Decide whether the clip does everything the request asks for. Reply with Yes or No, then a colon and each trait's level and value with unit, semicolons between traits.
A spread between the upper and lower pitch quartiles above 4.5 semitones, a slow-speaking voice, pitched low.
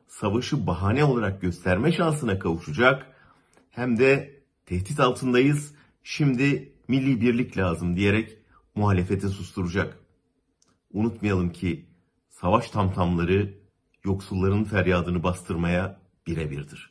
Yes: wide, 5.6 semitones; slow, 90 wpm; low, 100 Hz